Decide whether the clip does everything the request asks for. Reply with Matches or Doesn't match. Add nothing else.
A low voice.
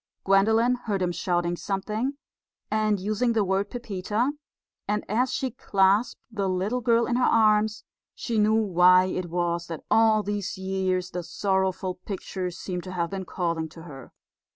Doesn't match